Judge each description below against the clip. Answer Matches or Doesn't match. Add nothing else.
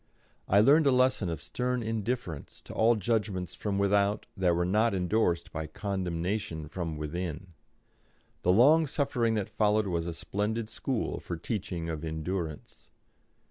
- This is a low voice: Matches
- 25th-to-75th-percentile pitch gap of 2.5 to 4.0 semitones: Doesn't match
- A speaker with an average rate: Matches